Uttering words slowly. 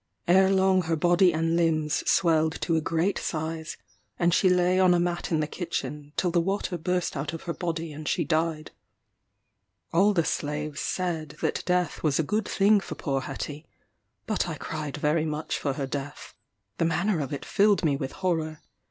No: average, 190 wpm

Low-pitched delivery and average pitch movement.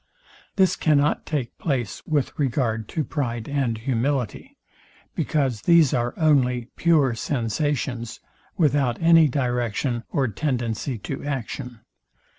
Yes: low, 130 Hz; average, 3.7 semitones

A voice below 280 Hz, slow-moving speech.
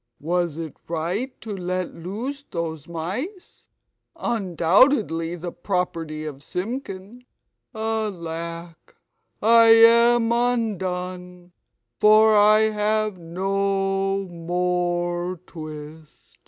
Yes: medium, 185 Hz; slow, 85 wpm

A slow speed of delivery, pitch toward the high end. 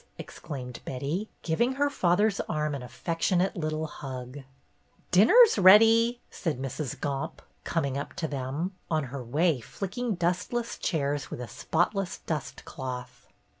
No: slow, 130 wpm; medium, 160 Hz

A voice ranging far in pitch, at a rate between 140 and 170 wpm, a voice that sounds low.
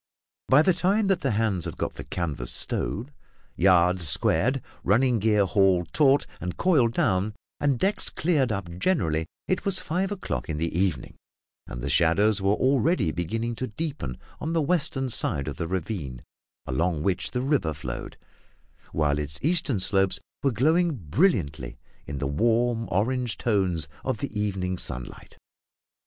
Yes: wide, 8.3 semitones; average, 155 wpm; low, 105 Hz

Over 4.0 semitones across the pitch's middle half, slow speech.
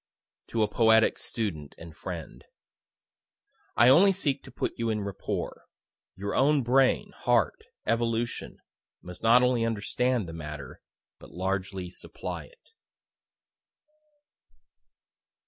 Yes: average, 4.7 semitones; slow, 110 wpm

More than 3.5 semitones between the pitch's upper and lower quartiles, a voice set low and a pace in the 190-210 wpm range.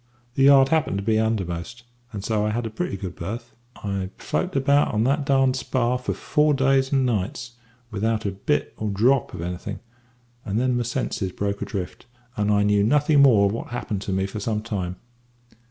Yes: average, 4.8 semitones; low, 110 Hz; average, 195 wpm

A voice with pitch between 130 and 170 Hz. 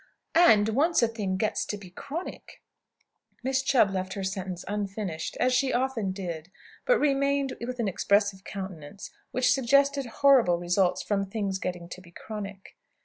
No: high, 205 Hz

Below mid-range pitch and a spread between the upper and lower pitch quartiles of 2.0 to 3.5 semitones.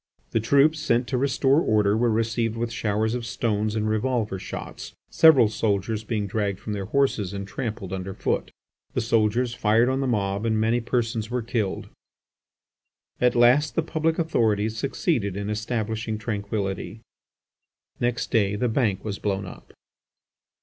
Yes: low, 110 Hz; average, 2.8 semitones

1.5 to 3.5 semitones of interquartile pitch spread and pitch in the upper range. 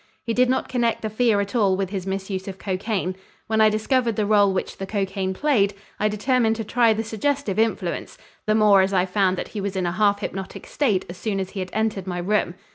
Yes: narrow, 2.6 semitones; high, 205 Hz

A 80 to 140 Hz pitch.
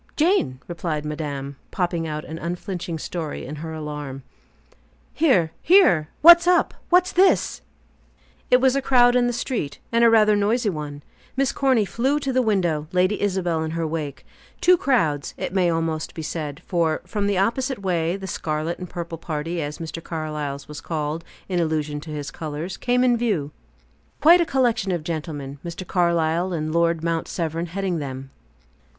No: medium, 170 Hz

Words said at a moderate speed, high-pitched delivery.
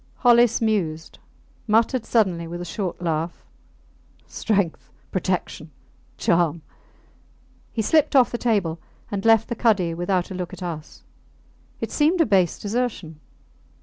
No: slow, 130 wpm; high, 195 Hz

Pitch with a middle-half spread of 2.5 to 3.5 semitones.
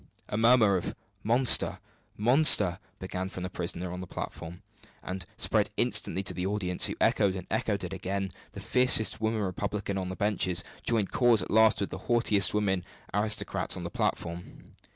Yes: average, 3.0 semitones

